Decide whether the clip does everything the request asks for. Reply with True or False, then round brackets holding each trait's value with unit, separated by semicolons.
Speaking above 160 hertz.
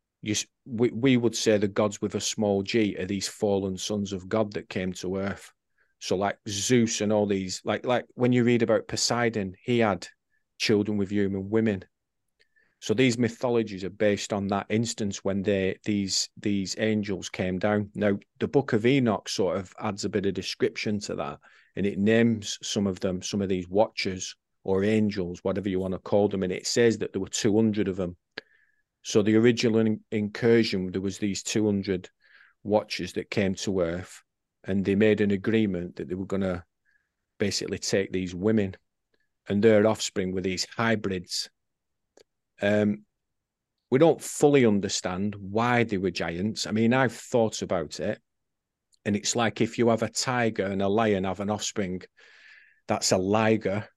False (105 Hz)